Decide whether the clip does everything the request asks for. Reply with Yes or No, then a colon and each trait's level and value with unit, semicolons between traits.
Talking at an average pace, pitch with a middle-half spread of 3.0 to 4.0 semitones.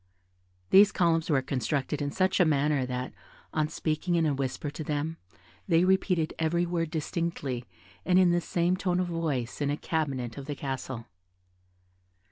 Yes: average, 165 wpm; average, 3.7 semitones